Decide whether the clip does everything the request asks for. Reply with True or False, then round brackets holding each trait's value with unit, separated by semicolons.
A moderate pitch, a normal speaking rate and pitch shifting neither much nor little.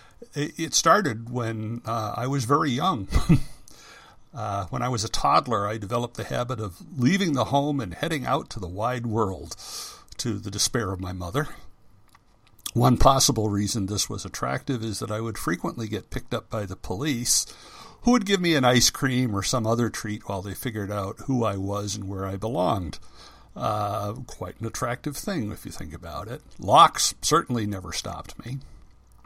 False (115 Hz; 185 wpm; 4.8 semitones)